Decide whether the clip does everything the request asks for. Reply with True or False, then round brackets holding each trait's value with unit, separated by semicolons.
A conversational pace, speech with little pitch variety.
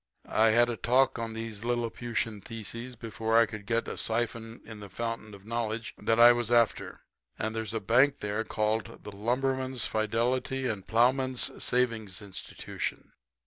True (160 wpm; 1.6 semitones)